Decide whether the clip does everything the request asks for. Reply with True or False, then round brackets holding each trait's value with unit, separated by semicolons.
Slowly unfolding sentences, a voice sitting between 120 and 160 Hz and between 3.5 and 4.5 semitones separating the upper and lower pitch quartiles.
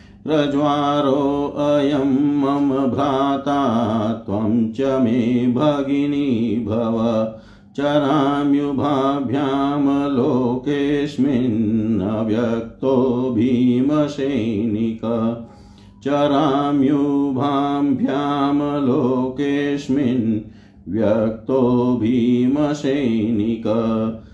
True (45 wpm; 135 Hz; 3.8 semitones)